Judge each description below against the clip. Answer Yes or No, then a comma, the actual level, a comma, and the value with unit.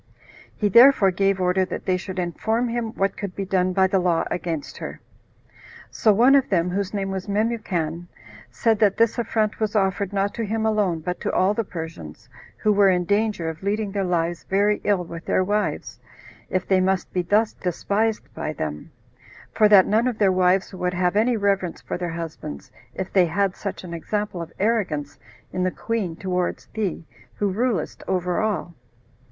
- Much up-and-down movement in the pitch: No, average, 2.8 semitones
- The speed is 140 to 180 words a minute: No, average, 190 wpm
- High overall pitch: Yes, high, 195 Hz